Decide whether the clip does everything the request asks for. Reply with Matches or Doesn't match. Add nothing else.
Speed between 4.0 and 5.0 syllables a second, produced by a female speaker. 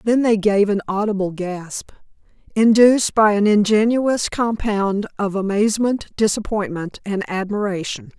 Matches